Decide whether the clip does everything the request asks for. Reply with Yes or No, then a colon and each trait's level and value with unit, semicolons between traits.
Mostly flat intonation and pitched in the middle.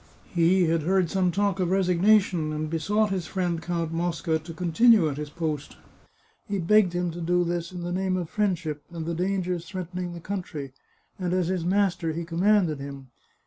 Yes: narrow, 2.3 semitones; medium, 175 Hz